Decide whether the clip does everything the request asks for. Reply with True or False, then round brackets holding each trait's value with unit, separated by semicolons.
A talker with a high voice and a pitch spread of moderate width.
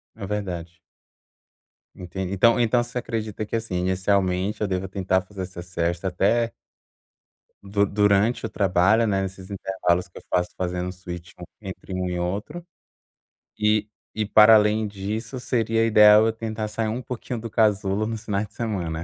False (100 Hz; 3.0 semitones)